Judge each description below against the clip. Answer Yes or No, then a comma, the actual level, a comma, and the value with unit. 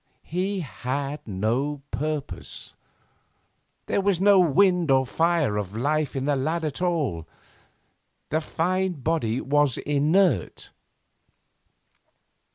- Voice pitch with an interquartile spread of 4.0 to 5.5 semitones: Yes, average, 4.6 semitones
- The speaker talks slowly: Yes, slow, 105 wpm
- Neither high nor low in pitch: Yes, medium, 150 Hz